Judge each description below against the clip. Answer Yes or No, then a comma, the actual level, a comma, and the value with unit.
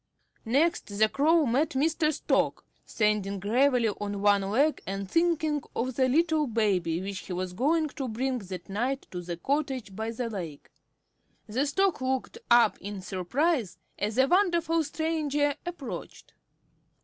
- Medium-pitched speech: No, very high, 255 Hz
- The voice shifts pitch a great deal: Yes, wide, 7.0 semitones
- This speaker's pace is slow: No, average, 150 wpm